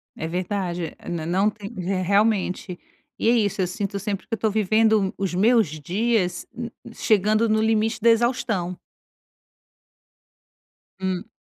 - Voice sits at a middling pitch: No, high, 205 Hz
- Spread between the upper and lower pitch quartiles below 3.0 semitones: No, average, 3.3 semitones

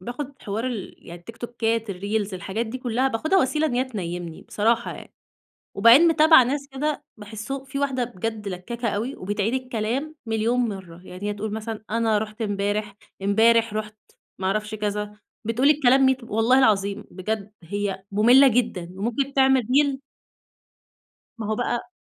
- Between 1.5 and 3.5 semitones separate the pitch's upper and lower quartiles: No, average, 3.9 semitones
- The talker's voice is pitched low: No, high, 225 Hz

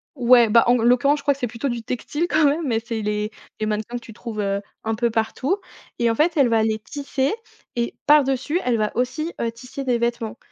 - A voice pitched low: No, high, 240 Hz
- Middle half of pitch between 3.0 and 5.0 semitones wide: Yes, average, 3.7 semitones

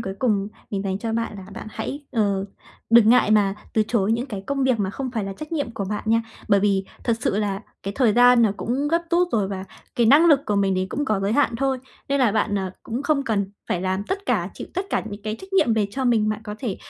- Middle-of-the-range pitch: No, high, 220 Hz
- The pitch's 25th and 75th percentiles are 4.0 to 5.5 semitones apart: Yes, average, 4.5 semitones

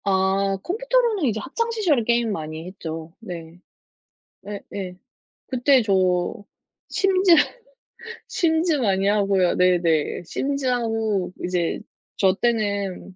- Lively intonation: Yes, wide, 6.7 semitones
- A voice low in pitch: No, high, 205 Hz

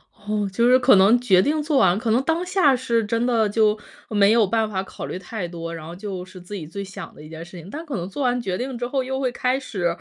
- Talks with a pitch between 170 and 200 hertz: No, high, 215 Hz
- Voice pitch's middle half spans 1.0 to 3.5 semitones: No, average, 5.2 semitones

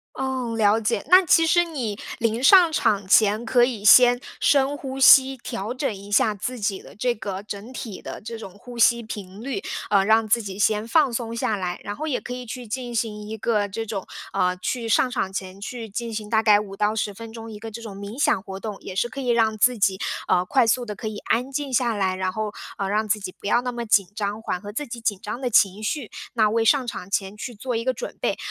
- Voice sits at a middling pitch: No, high, 225 Hz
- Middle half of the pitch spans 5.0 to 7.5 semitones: No, average, 3.2 semitones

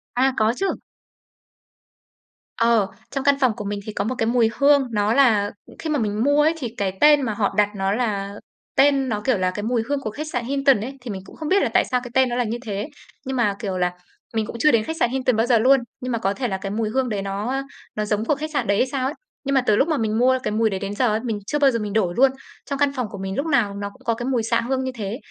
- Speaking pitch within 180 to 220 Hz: No, high, 235 Hz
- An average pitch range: Yes, average, 4.4 semitones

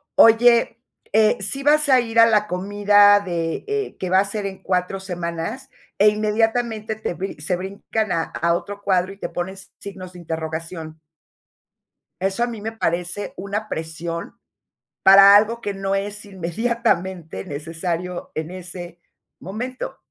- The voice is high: Yes, high, 195 Hz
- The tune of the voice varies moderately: Yes, average, 3.6 semitones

